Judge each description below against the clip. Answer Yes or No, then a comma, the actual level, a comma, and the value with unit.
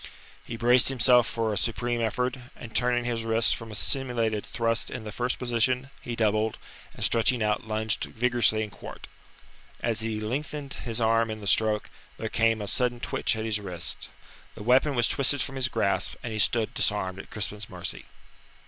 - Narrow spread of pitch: Yes, narrow, 2.1 semitones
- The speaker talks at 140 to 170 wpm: No, average, 185 wpm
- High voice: No, low, 115 Hz